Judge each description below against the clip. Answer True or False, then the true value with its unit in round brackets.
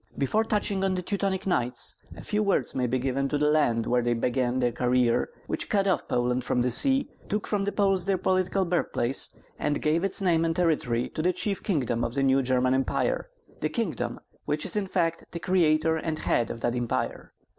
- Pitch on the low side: False (155 Hz)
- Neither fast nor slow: False (210 wpm)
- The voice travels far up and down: True (7.3 semitones)